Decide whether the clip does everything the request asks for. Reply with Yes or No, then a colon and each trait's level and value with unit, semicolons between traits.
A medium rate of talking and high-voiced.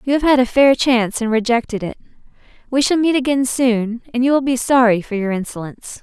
No: fast, 220 wpm; high, 245 Hz